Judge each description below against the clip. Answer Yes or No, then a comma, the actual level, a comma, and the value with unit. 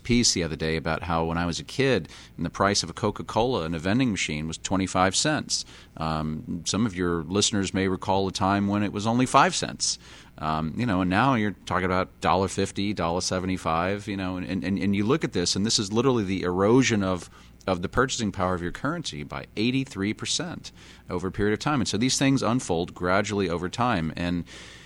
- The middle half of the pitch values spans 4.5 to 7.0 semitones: No, average, 3.3 semitones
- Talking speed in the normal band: No, fast, 225 wpm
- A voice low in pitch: Yes, very low, 95 Hz